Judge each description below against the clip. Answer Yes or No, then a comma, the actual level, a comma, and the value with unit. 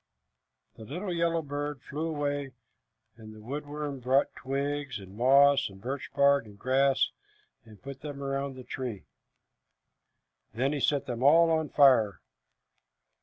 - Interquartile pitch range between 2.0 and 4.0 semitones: Yes, narrow, 2.4 semitones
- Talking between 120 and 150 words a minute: Yes, average, 145 wpm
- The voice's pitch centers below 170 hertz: Yes, medium, 140 Hz